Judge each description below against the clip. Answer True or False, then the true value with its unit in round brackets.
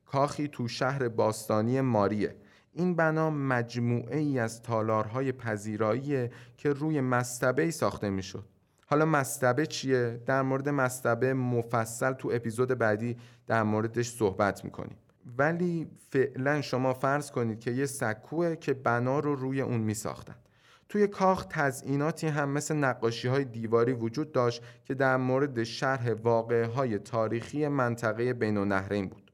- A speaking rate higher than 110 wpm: True (140 wpm)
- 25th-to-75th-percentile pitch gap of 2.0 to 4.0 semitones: True (3.5 semitones)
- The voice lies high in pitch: False (125 Hz)